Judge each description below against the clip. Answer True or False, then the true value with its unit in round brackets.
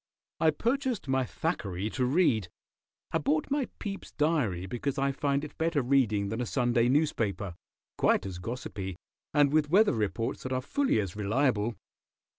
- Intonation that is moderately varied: False (6.1 semitones)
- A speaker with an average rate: True (160 wpm)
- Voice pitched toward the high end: False (130 Hz)